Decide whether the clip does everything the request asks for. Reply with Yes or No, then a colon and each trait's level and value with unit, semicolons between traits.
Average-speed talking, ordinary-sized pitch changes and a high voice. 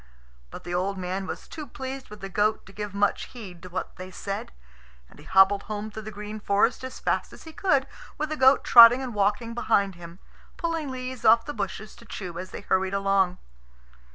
No: fast, 210 wpm; average, 4.5 semitones; high, 210 Hz